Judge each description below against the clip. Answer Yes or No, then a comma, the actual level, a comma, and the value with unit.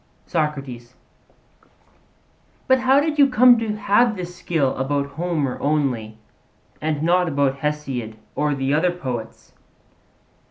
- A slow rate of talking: Yes, slow, 120 wpm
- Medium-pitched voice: Yes, medium, 150 Hz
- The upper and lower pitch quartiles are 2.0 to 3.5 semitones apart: No, average, 5.1 semitones